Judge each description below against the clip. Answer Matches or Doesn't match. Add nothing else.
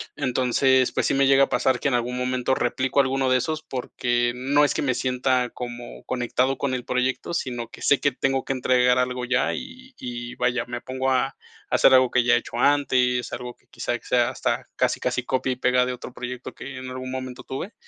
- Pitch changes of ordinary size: Doesn't match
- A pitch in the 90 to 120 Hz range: Doesn't match